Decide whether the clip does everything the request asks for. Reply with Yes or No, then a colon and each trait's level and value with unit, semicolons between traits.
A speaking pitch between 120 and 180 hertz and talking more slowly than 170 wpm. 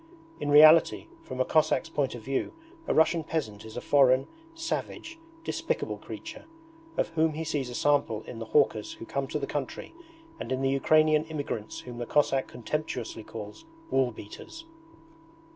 Yes: medium, 140 Hz; average, 160 wpm